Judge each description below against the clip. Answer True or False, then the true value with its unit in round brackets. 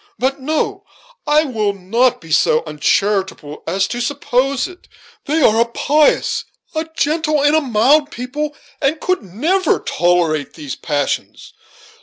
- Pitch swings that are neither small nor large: False (7.7 semitones)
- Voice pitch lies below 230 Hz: False (255 Hz)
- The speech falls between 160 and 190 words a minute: False (140 wpm)